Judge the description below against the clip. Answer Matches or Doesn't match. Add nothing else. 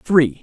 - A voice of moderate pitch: Matches